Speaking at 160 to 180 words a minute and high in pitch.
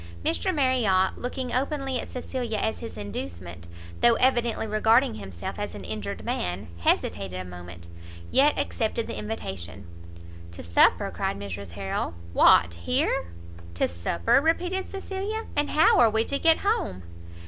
No: average, 145 wpm; high, 215 Hz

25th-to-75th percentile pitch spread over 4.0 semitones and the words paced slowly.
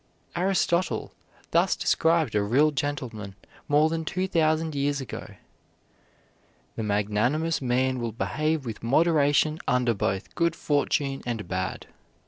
Yes: average, 5.3 semitones; slow, 120 wpm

